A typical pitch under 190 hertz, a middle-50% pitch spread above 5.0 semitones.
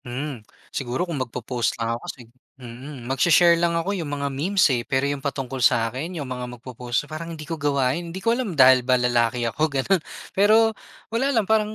Yes: medium, 140 Hz; wide, 5.4 semitones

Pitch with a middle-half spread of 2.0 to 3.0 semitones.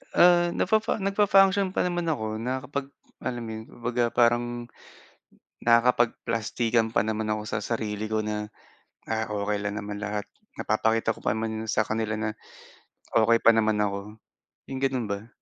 Yes: narrow, 2.6 semitones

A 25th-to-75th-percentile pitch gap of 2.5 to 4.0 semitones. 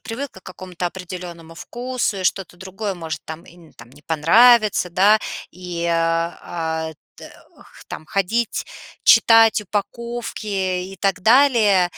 No: average, 4.7 semitones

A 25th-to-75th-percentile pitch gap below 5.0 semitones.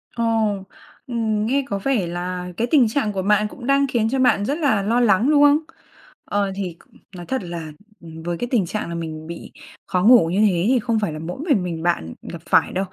No: wide, 5.6 semitones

